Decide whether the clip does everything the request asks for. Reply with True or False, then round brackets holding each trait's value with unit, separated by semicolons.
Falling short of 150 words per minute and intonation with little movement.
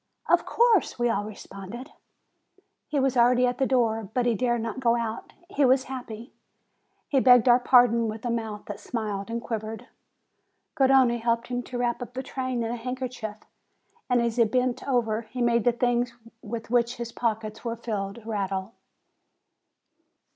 False (170 wpm; 2.0 semitones)